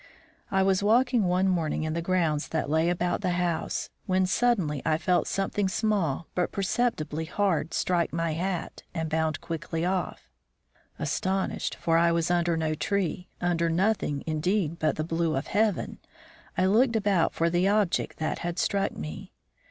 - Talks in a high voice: No, medium, 175 Hz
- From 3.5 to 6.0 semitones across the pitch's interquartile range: No, average, 3.1 semitones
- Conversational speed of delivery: Yes, average, 165 wpm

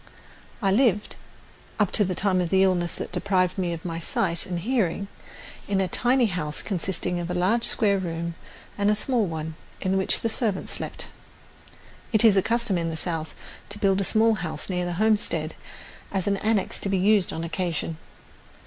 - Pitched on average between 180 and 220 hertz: Yes, high, 190 Hz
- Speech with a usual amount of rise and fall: Yes, average, 3.3 semitones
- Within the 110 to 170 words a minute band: No, average, 190 wpm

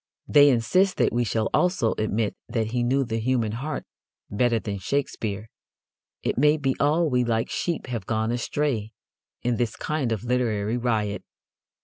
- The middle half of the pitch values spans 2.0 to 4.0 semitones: Yes, average, 3.5 semitones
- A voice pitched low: Yes, low, 120 Hz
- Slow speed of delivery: No, average, 160 wpm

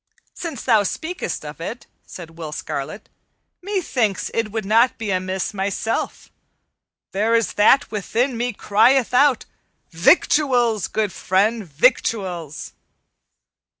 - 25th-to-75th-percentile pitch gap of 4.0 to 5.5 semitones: Yes, average, 4.4 semitones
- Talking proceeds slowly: Yes, slow, 115 wpm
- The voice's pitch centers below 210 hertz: No, high, 220 Hz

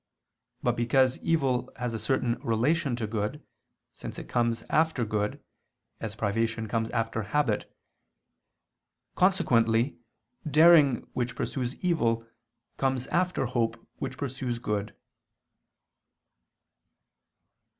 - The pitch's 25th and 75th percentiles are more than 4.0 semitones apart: No, average, 3.2 semitones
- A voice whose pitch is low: Yes, low, 120 Hz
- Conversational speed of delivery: No, slow, 100 wpm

